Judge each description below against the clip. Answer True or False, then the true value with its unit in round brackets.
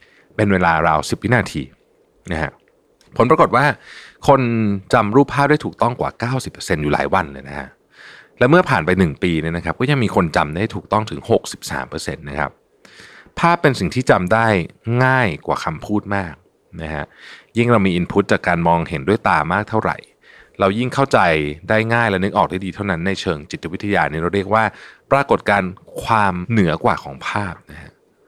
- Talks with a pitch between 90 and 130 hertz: True (100 Hz)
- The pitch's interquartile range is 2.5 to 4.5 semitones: False (5.2 semitones)